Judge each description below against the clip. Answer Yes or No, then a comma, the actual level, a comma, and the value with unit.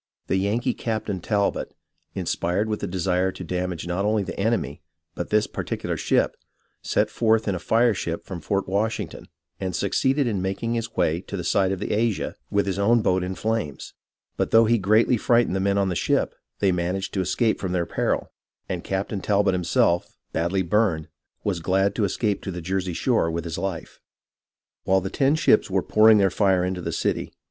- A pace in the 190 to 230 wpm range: Yes, average, 195 wpm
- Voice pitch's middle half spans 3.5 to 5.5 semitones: No, average, 3.1 semitones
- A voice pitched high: No, very low, 95 Hz